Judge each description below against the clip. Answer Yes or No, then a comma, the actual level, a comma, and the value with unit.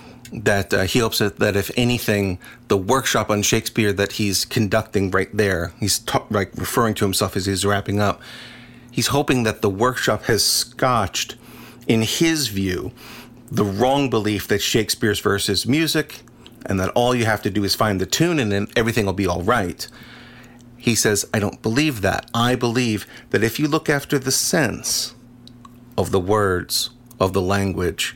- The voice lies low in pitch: Yes, low, 115 Hz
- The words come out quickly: No, average, 175 wpm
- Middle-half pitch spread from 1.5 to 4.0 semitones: Yes, average, 3.4 semitones